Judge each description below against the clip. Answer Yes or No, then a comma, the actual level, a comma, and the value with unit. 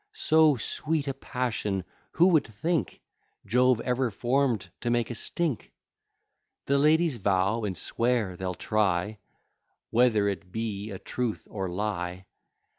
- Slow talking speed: Yes, slow, 130 wpm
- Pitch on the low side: Yes, low, 115 Hz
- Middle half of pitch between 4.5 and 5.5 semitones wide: Yes, average, 5.0 semitones